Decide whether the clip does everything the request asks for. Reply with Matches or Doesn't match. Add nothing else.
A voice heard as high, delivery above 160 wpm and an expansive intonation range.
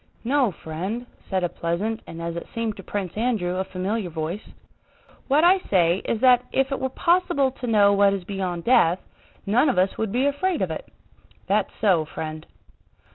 Matches